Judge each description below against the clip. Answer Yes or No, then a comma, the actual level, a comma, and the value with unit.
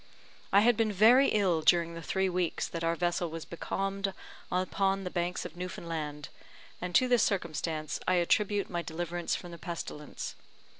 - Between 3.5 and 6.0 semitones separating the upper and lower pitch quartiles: No, average, 2.7 semitones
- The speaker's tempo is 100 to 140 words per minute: No, average, 165 wpm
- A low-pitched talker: No, medium, 175 Hz